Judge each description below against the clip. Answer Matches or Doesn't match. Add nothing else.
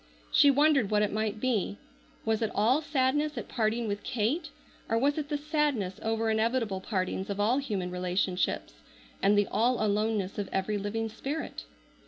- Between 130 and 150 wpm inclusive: Doesn't match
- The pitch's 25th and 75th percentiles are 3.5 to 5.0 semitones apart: Matches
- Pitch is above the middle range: Matches